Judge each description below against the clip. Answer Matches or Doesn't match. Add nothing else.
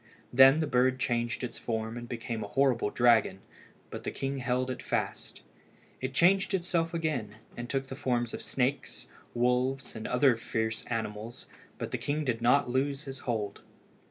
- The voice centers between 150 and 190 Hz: Doesn't match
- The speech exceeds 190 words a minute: Doesn't match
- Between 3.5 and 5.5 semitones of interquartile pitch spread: Doesn't match